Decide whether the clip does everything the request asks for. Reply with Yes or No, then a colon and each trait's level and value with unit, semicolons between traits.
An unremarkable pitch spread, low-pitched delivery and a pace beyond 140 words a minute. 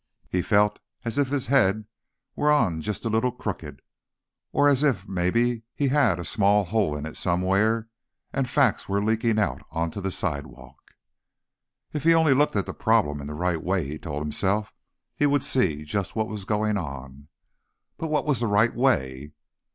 No: wide, 6.0 semitones; low, 105 Hz; average, 180 wpm